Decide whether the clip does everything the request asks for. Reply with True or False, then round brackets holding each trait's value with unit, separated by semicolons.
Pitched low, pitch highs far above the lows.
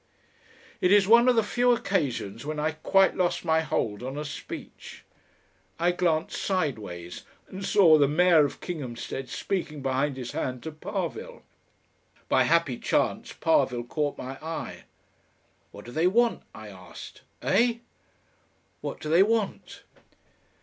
False (160 Hz; 6.5 semitones)